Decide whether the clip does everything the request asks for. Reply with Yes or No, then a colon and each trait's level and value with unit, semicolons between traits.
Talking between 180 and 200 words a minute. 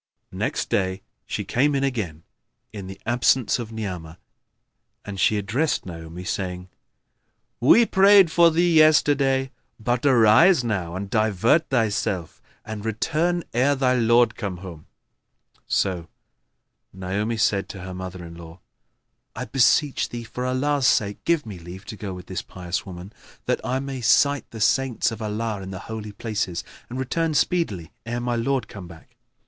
No: average, 155 wpm